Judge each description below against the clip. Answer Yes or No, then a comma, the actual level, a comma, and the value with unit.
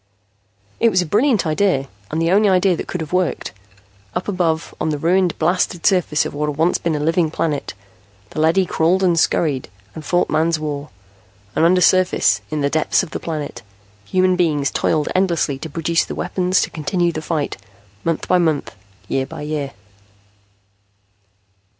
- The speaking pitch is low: No, medium, 165 Hz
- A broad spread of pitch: No, average, 3.0 semitones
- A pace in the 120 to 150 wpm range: No, average, 175 wpm